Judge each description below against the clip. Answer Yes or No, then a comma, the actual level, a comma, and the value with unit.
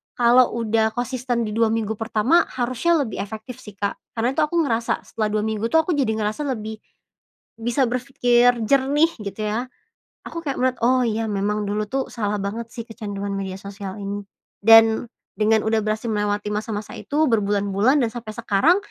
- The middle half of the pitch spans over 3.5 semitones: No, average, 3.0 semitones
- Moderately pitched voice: No, high, 225 Hz